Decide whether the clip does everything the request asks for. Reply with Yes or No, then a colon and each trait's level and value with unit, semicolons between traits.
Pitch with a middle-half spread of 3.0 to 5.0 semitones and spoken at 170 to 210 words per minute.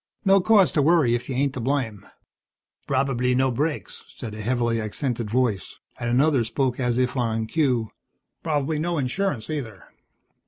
No: average, 3.8 semitones; average, 160 wpm